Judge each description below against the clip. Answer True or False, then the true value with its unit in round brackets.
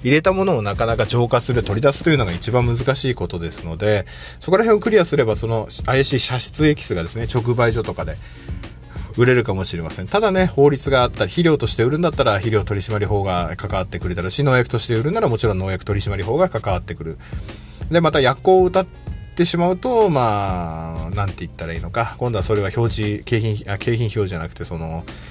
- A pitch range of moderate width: False (5.9 semitones)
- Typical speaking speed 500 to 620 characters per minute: False (450 characters per minute)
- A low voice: True (110 Hz)